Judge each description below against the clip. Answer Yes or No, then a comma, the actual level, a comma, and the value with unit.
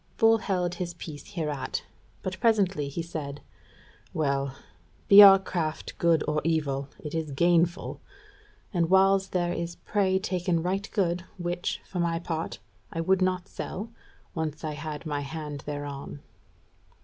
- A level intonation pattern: No, average, 3.5 semitones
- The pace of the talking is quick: No, average, 145 wpm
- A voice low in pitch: No, medium, 170 Hz